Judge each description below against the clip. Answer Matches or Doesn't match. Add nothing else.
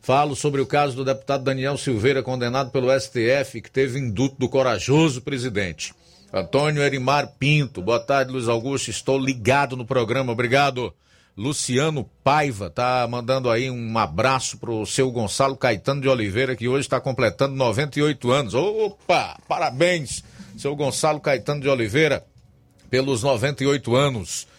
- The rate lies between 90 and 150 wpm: Matches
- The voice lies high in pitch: Doesn't match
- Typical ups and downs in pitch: Doesn't match